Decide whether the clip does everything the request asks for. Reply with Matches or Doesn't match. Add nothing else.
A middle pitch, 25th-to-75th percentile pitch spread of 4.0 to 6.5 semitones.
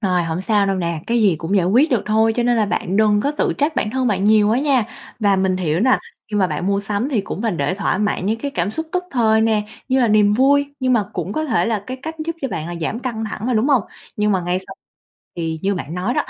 Doesn't match